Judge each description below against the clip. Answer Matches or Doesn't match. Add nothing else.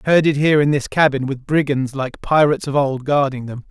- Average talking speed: Doesn't match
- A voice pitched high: Doesn't match